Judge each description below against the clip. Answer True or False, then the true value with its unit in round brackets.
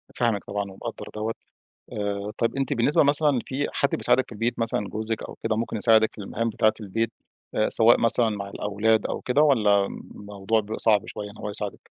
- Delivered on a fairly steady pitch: True (2.2 semitones)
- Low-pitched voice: True (110 Hz)